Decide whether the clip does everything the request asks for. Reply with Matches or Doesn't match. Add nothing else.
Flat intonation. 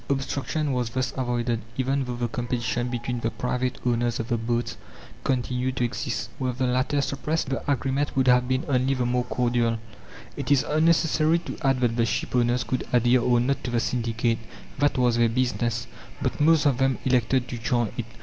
Matches